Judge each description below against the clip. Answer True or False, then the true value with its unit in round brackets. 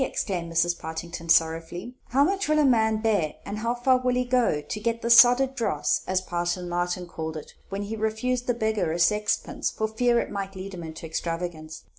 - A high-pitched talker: True (200 Hz)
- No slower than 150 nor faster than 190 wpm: False (205 wpm)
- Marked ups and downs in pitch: True (5.8 semitones)